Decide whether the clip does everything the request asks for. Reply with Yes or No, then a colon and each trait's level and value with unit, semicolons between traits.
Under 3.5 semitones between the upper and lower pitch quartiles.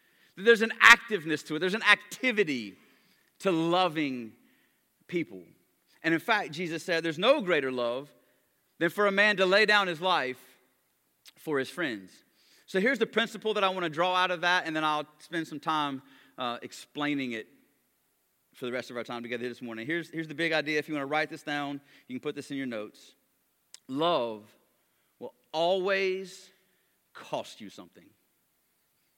No: average, 5.1 semitones